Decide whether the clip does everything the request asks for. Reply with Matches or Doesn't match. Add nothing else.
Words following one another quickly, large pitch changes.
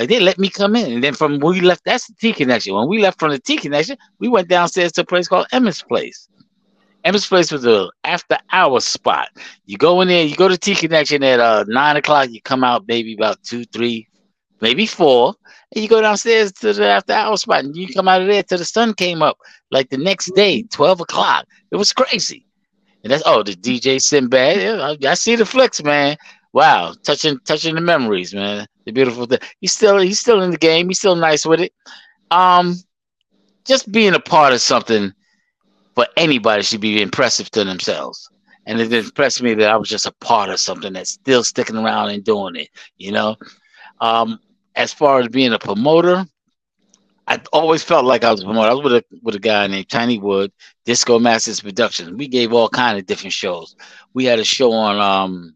Matches